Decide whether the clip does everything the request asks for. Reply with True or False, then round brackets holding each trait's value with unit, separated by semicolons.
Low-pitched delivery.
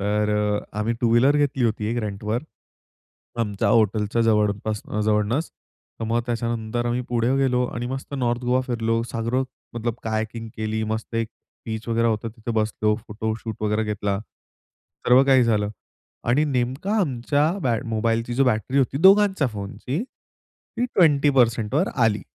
True (115 Hz)